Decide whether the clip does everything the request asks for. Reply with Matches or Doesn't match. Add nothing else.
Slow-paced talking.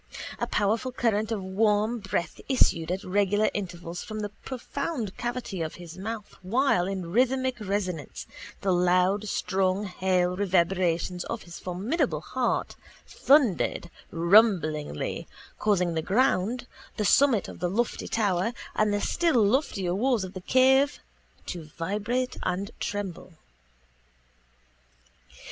Matches